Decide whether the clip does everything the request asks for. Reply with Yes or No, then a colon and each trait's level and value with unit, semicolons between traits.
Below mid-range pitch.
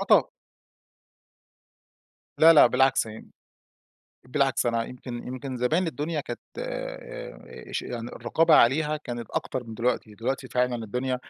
Yes: low, 125 Hz